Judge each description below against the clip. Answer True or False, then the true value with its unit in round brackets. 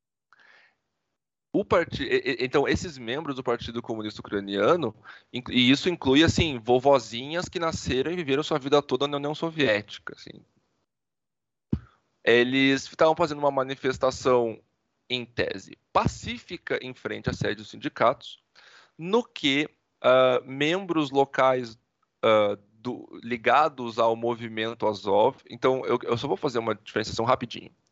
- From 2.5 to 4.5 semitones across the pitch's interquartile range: True (3.7 semitones)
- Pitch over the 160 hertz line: False (130 Hz)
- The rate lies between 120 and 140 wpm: True (125 wpm)